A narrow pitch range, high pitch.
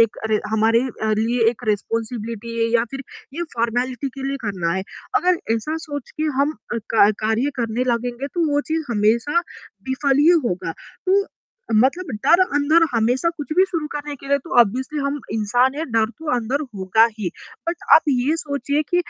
No: average, 4.7 semitones; very high, 250 Hz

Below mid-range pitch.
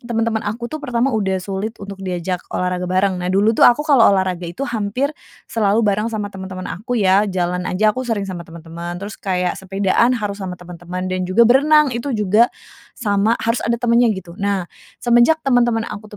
No: high, 200 Hz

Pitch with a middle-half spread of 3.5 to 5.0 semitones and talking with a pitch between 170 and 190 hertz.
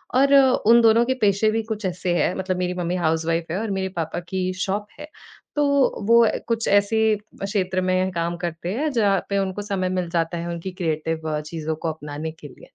Yes: average, 4.1 semitones; medium, 185 Hz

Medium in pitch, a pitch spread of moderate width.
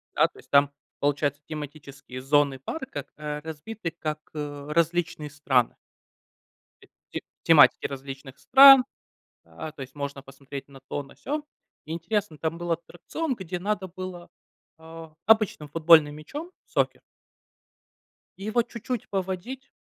Yes: medium, 160 Hz; average, 4.7 semitones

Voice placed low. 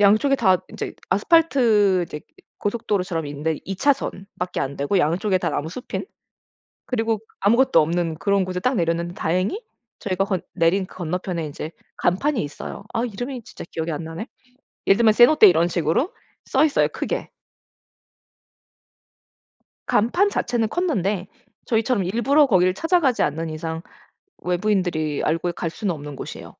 No: high, 190 Hz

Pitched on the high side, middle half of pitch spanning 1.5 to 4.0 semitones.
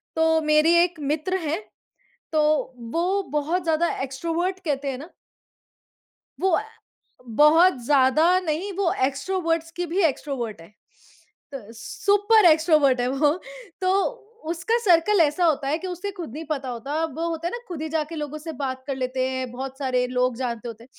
No: very high, 310 Hz; average, 4.4 semitones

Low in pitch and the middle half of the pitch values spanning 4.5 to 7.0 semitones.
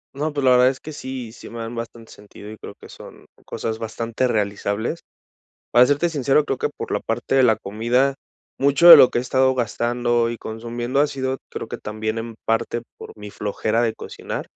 No: low, 120 Hz; average, 2.8 semitones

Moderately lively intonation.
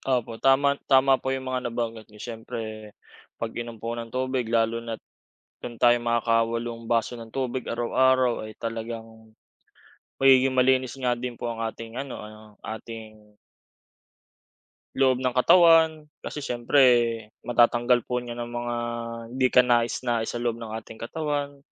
No: narrow, 2.1 semitones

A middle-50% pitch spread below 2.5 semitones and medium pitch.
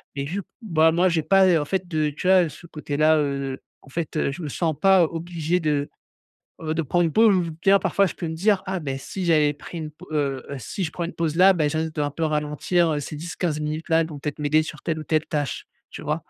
No: average, 2.8 semitones; medium, 160 Hz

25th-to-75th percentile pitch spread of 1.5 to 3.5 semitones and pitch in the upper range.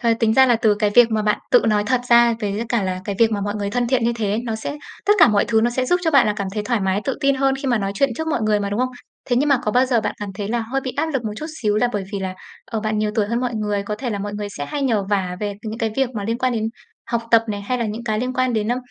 Yes: average, 3.1 semitones; high, 225 Hz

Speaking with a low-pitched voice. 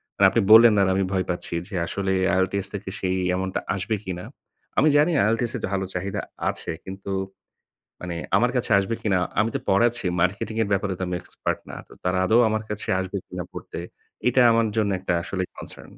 Yes: low, 100 Hz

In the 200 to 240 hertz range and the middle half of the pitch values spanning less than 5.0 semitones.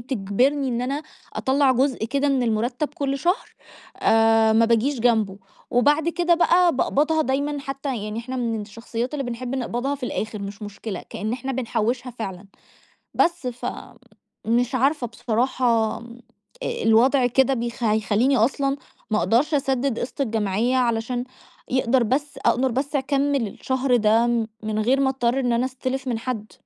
No: very high, 250 Hz; average, 3.3 semitones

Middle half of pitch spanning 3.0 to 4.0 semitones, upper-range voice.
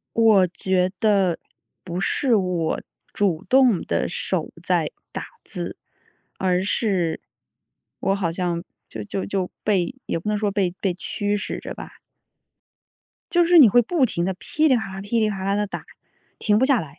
Yes: average, 3.3 semitones; high, 195 Hz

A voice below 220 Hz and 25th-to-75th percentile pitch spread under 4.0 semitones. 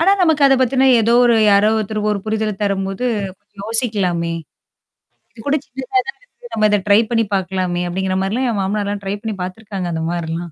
Yes: high, 210 Hz; average, 3.6 semitones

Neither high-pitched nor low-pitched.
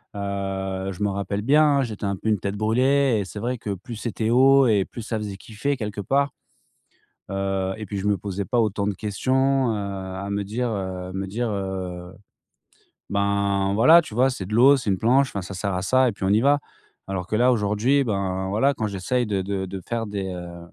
No: low, 105 Hz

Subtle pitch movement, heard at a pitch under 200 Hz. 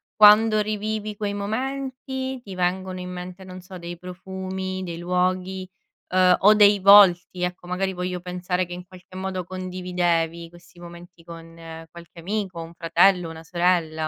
Yes: narrow, 1.8 semitones; medium, 185 Hz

